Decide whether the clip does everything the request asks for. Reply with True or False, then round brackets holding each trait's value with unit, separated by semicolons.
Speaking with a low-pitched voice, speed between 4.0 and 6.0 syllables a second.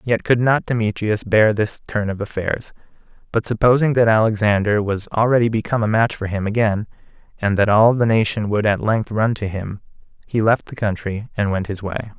True (110 Hz; 5.4 syllables/s)